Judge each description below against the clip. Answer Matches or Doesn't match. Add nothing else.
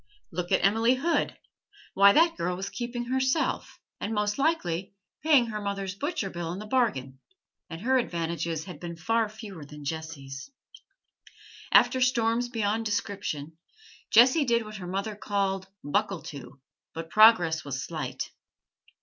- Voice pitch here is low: Doesn't match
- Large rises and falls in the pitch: Matches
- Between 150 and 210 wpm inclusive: Doesn't match